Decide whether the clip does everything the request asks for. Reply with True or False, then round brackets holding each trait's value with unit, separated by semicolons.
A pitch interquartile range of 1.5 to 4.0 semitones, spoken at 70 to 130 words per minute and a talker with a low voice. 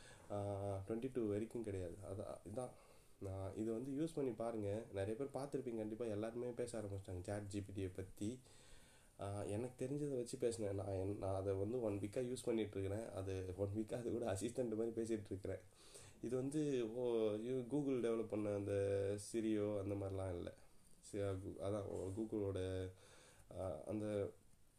False (3.4 semitones; 140 wpm; 105 Hz)